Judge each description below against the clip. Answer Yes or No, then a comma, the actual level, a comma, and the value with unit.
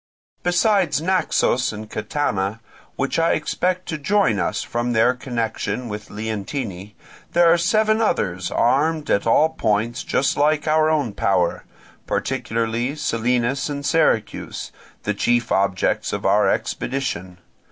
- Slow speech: Yes, slow, 130 wpm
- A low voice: Yes, low, 125 Hz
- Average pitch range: No, wide, 6.3 semitones